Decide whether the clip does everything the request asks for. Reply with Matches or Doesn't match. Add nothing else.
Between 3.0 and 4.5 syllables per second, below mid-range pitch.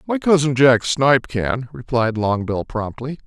Matches